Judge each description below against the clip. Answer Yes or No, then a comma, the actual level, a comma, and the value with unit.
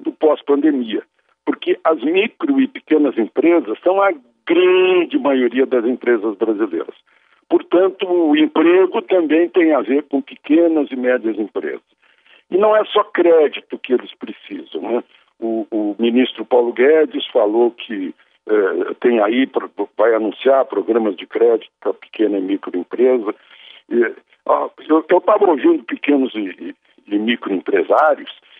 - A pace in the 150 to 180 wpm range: No, average, 130 wpm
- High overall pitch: Yes, high, 200 Hz